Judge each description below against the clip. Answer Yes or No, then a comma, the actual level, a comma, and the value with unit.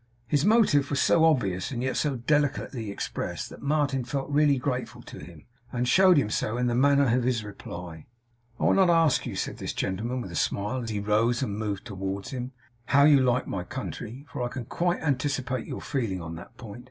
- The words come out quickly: Yes, fast, 215 wpm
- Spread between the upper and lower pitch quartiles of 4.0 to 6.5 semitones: Yes, average, 5.1 semitones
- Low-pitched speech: Yes, low, 125 Hz